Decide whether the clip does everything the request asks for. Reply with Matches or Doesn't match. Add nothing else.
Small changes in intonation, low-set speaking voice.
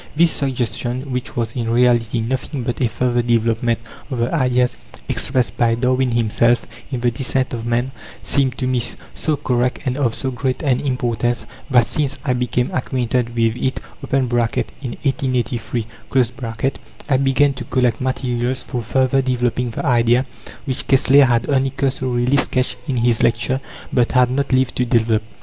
Matches